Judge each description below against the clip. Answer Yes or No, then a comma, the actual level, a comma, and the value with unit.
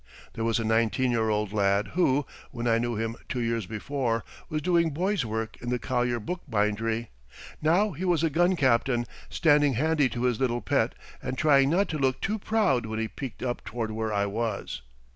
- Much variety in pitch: No, average, 5.0 semitones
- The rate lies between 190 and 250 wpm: Yes, average, 200 wpm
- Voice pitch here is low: Yes, low, 120 Hz